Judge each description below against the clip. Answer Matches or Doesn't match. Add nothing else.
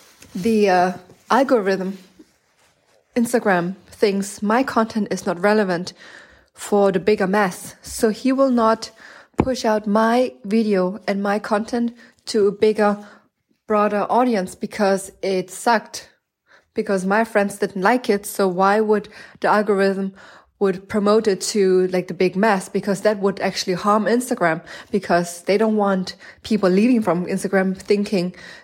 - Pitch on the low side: Doesn't match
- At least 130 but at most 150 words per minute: Matches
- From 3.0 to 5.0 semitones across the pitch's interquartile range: Doesn't match